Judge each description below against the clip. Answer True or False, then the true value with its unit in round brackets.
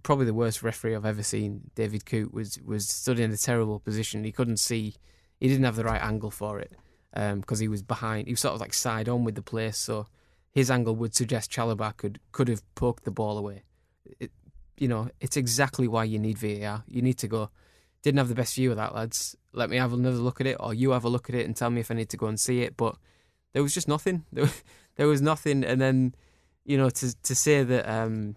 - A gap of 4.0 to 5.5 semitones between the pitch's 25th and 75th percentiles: False (2.9 semitones)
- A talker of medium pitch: False (115 Hz)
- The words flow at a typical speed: False (255 wpm)